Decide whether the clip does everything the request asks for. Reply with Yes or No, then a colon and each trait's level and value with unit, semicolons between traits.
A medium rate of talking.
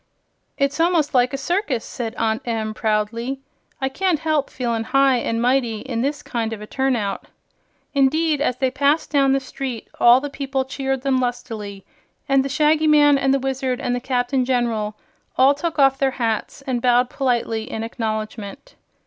Yes: average, 180 wpm